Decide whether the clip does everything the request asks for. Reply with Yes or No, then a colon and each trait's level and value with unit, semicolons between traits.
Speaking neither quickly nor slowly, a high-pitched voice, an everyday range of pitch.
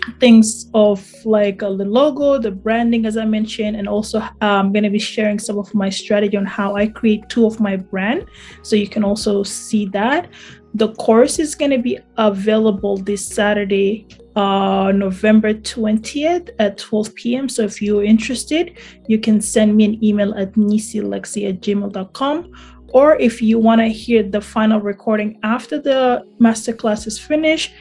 No: average, 175 wpm; high, 215 Hz; narrow, 2.1 semitones